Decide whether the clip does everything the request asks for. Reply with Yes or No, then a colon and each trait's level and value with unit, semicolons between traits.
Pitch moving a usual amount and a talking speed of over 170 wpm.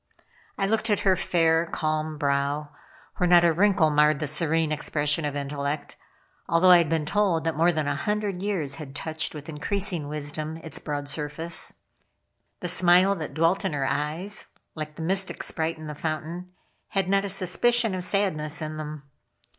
Yes: average, 3.3 semitones; average, 180 wpm